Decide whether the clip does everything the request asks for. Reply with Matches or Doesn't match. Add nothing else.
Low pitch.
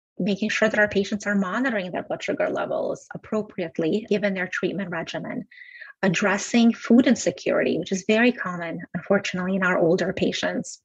Doesn't match